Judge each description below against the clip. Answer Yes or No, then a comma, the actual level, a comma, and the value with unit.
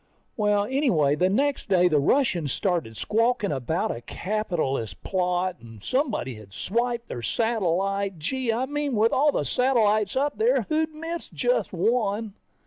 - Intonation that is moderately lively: No, wide, 6.8 semitones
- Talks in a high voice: Yes, high, 210 Hz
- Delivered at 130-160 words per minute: Yes, average, 150 wpm